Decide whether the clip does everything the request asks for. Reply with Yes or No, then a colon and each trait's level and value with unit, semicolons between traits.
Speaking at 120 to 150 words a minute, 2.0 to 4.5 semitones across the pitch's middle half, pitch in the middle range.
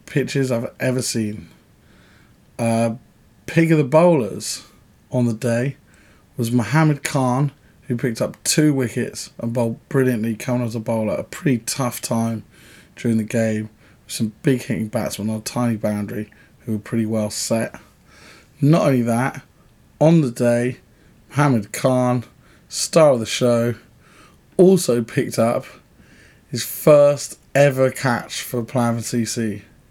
No: average, 140 wpm; average, 2.9 semitones; low, 120 Hz